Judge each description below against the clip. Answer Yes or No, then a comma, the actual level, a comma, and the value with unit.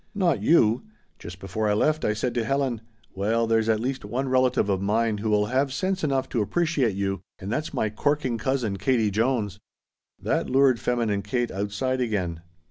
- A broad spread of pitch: No, average, 4.2 semitones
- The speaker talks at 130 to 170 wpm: No, average, 185 wpm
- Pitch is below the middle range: Yes, low, 115 Hz